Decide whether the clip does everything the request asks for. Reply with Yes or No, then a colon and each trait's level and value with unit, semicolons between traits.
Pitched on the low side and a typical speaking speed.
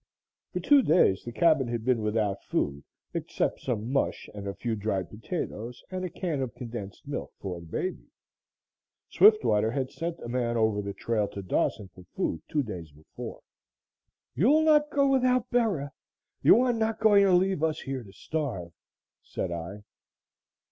Yes: low, 125 Hz; average, 170 wpm